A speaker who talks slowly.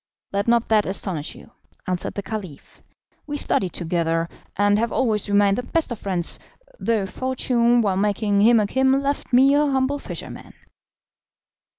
No: average, 160 wpm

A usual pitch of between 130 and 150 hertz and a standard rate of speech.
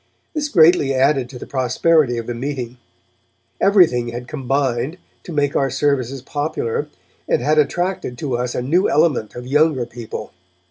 Yes: low, 135 Hz; average, 155 wpm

